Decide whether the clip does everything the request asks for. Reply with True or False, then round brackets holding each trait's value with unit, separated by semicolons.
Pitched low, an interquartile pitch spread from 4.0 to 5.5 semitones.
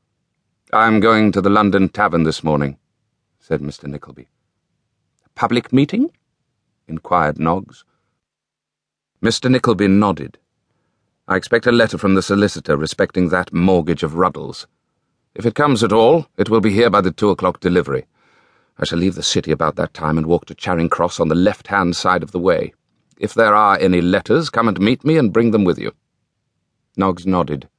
True (95 Hz; 5.0 semitones)